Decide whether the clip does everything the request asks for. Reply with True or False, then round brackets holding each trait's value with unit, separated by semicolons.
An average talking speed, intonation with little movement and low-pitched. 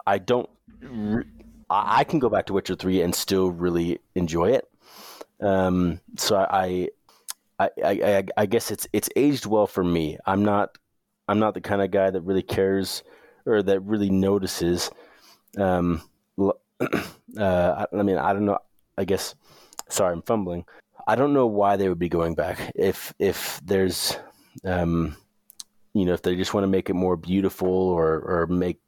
True (170 wpm; 2.3 semitones; 95 Hz)